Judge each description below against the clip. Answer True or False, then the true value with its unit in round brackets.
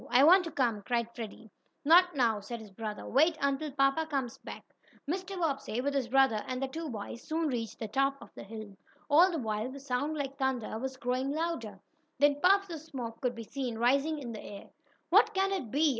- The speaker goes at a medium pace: False (215 wpm)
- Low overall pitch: False (270 Hz)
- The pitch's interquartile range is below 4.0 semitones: False (5.1 semitones)